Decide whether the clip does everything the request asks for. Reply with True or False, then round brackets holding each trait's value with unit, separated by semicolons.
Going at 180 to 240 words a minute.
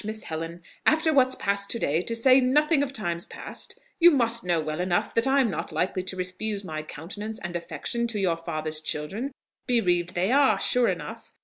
True (195 wpm)